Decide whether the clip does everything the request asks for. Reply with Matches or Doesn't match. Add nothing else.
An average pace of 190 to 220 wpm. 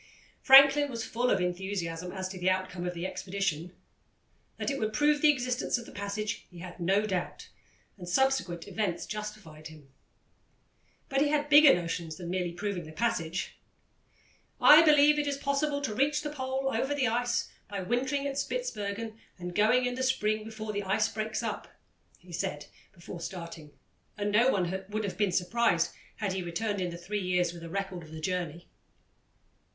Doesn't match